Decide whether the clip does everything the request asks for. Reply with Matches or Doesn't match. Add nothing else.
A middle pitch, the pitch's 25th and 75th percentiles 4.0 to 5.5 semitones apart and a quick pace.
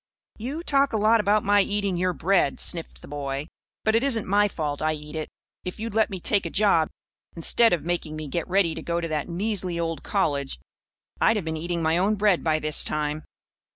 Matches